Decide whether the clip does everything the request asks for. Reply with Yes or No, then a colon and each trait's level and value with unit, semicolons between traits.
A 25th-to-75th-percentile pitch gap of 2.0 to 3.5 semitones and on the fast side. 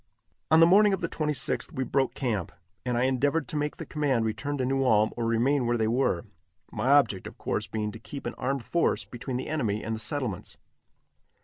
No: average, 4.1 semitones; fast, 215 wpm